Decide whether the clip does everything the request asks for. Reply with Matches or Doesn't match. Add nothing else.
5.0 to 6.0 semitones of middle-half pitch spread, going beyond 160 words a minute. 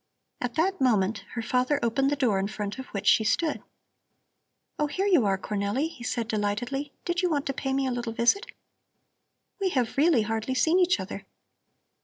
Matches